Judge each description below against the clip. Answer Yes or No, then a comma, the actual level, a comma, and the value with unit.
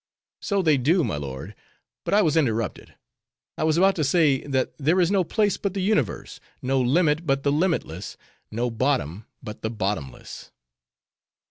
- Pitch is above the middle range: No, medium, 140 Hz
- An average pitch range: No, wide, 7.3 semitones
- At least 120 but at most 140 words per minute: No, average, 165 wpm